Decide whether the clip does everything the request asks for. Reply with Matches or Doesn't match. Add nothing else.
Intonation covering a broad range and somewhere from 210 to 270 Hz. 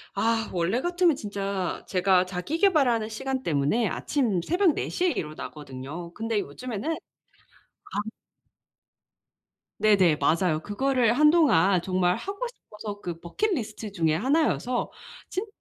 Matches